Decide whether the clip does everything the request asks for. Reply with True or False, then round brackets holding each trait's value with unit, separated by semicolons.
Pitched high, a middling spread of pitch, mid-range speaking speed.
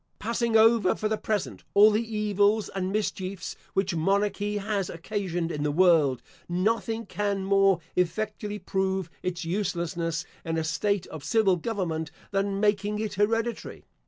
True (195 Hz; 3.1 semitones; 145 wpm)